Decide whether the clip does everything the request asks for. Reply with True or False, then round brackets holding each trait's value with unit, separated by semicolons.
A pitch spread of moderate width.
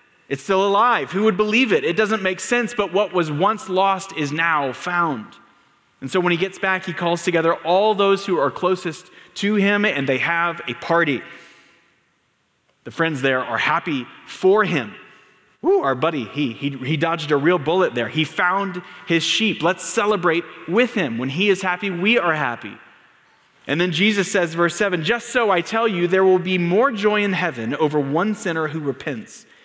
True (3.7 semitones)